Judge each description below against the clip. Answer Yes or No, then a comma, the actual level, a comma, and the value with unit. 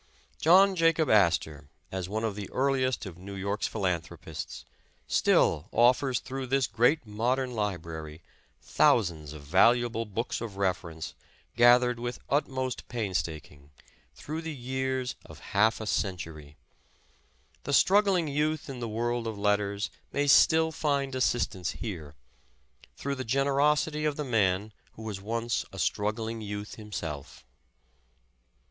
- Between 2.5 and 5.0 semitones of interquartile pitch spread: No, wide, 5.4 semitones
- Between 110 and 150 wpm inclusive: Yes, slow, 135 wpm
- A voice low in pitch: Yes, low, 115 Hz